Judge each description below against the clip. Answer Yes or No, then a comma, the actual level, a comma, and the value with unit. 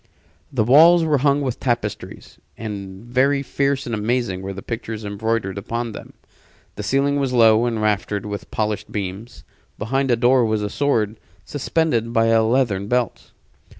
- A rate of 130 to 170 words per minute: Yes, average, 160 wpm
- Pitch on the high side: No, low, 115 Hz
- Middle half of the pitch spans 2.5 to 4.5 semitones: Yes, average, 3.9 semitones